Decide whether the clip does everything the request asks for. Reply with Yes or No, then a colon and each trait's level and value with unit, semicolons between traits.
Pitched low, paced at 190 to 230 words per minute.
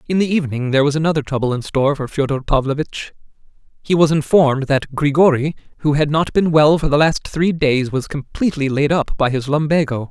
No: medium, 145 Hz; average, 200 wpm